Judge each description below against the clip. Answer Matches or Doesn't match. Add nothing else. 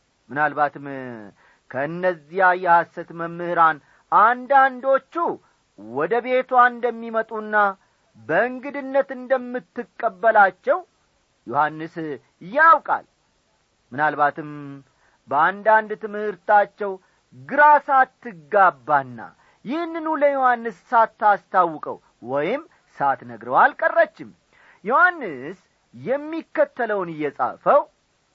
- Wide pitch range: Matches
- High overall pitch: Matches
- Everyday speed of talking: Doesn't match